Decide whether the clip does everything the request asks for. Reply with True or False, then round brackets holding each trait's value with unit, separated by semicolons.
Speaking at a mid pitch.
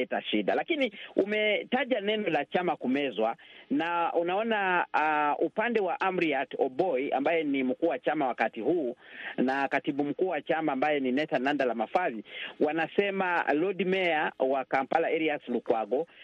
True (165 Hz)